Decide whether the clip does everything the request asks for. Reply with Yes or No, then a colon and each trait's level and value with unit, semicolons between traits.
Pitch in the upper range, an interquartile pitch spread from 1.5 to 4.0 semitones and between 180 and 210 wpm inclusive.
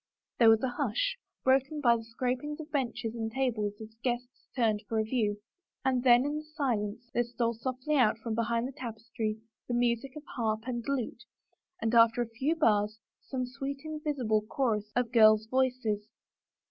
Yes: high, 240 Hz; average, 2.9 semitones; average, 185 wpm